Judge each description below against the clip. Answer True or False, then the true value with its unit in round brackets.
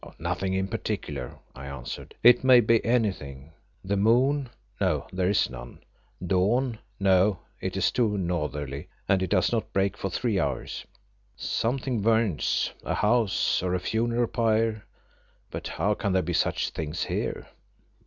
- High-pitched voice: False (100 Hz)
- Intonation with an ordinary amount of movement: True (4.3 semitones)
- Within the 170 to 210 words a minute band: False (150 wpm)